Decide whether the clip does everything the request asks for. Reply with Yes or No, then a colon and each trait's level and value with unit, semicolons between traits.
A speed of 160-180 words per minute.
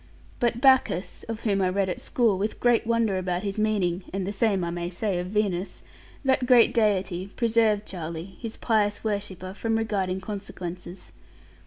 Yes: average, 170 wpm